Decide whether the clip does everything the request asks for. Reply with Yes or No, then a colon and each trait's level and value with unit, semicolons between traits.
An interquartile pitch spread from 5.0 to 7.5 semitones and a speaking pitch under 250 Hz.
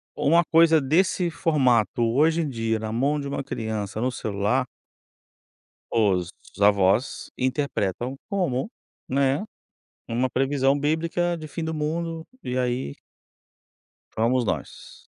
Yes: wide, 5.5 semitones; low, 135 Hz